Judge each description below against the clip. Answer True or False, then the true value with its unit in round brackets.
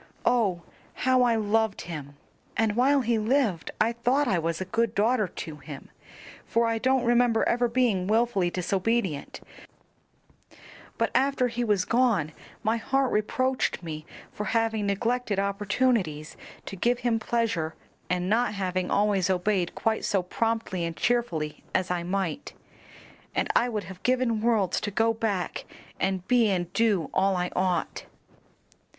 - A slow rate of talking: False (150 wpm)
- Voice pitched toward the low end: False (215 Hz)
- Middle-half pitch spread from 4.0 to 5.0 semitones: True (4.6 semitones)